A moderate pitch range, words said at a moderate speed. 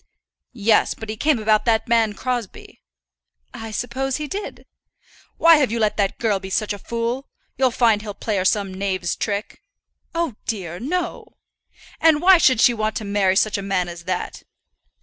Yes: average, 4.2 semitones; average, 180 wpm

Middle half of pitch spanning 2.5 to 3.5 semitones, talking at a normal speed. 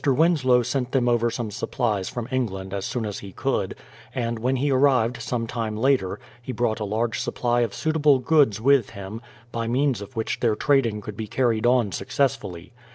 Yes: average, 3.1 semitones; average, 190 wpm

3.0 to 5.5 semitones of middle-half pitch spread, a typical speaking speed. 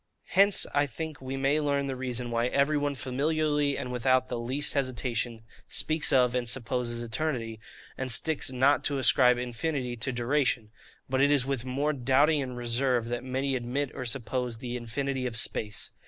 No: narrow, 2.6 semitones; average, 175 wpm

